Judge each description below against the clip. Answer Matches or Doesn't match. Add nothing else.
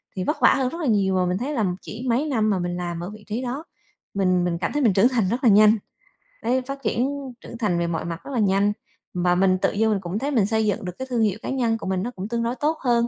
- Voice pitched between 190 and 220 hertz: Matches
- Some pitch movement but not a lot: Matches